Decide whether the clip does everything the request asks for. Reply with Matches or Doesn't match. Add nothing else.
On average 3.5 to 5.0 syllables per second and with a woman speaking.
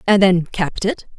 Matches